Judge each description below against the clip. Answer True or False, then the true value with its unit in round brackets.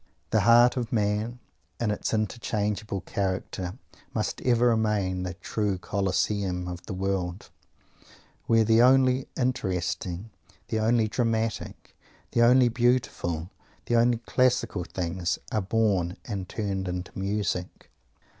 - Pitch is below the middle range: True (105 Hz)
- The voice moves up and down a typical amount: True (4.0 semitones)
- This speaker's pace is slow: True (120 wpm)